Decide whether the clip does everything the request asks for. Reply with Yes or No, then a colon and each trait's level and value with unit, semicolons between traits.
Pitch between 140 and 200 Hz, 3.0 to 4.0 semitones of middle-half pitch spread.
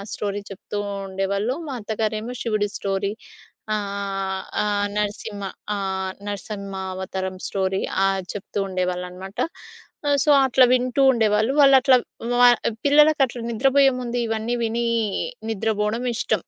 No: high, 210 Hz; average, 3.6 semitones